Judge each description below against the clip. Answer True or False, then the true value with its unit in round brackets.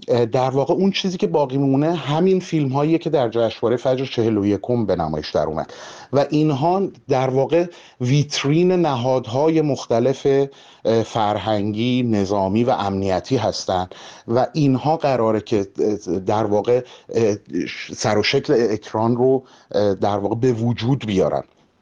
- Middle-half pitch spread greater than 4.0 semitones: True (4.8 semitones)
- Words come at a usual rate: True (130 wpm)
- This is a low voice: True (130 Hz)